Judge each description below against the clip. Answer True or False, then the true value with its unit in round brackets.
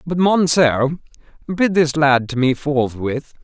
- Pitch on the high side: False (150 Hz)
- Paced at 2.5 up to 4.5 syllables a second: True (3.6 syllables/s)